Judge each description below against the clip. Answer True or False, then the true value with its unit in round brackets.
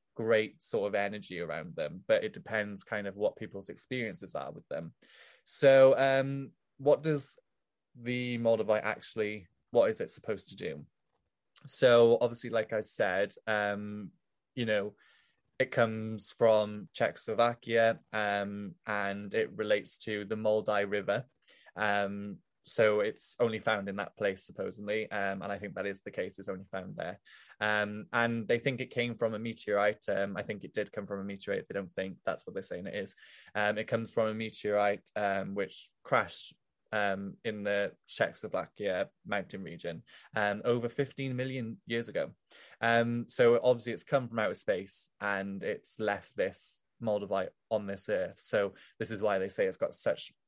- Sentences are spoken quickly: False (170 wpm)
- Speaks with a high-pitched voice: False (110 Hz)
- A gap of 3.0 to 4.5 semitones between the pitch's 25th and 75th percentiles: False (2.5 semitones)